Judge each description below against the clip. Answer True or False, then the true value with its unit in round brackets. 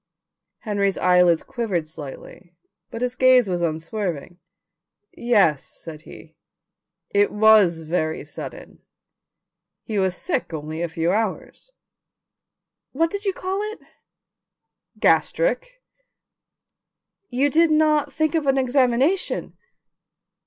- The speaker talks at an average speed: False (105 wpm)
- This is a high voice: True (215 Hz)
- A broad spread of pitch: True (8.9 semitones)